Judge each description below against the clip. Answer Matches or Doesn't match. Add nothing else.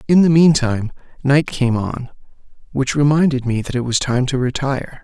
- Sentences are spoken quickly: Doesn't match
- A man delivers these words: Matches